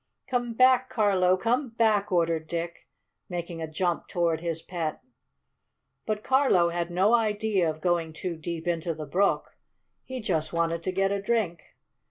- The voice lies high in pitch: No, medium, 180 Hz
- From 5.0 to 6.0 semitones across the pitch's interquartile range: No, average, 4.2 semitones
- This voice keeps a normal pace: Yes, average, 160 wpm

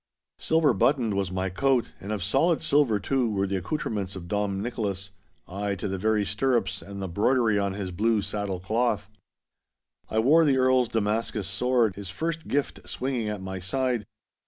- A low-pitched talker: Yes, low, 105 Hz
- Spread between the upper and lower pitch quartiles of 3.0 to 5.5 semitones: Yes, average, 4.4 semitones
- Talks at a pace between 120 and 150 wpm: No, average, 170 wpm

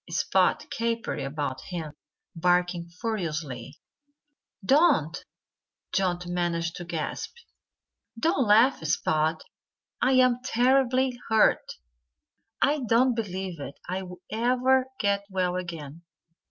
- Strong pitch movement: Yes, wide, 6.4 semitones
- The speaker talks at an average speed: No, slow, 90 wpm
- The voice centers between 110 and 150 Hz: No, medium, 185 Hz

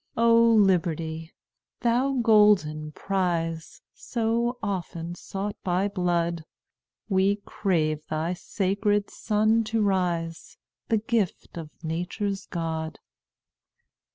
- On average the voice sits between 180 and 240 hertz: Yes, high, 190 Hz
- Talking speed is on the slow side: Yes, slow, 95 wpm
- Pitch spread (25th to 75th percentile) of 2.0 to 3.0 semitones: No, average, 4.1 semitones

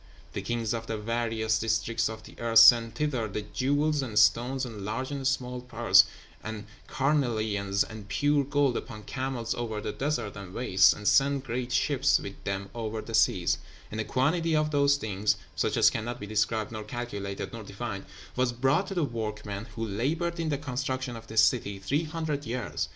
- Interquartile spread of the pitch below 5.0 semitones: Yes, average, 4.0 semitones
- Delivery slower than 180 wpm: No, average, 190 wpm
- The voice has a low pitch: Yes, low, 115 Hz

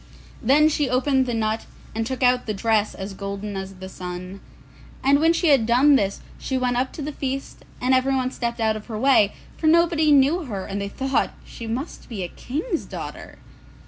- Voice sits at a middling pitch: No, very high, 250 Hz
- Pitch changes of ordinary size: Yes, average, 4.6 semitones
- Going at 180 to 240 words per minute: Yes, fast, 205 wpm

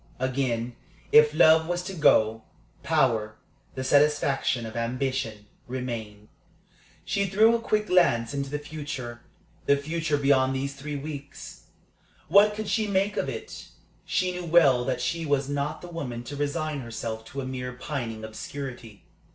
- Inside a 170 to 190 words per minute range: No, average, 150 wpm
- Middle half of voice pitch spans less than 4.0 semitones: No, average, 4.5 semitones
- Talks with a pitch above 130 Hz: Yes, medium, 140 Hz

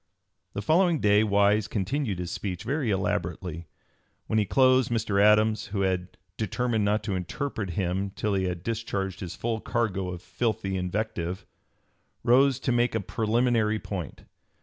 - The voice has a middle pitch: No, low, 105 Hz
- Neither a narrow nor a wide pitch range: Yes, average, 3.6 semitones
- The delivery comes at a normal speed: Yes, average, 150 wpm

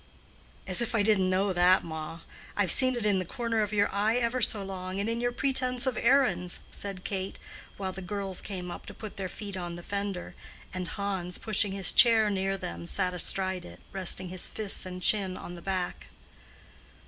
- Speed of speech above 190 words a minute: Yes, fast, 205 wpm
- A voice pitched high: Yes, high, 195 Hz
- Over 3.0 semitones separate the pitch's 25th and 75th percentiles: No, narrow, 2.6 semitones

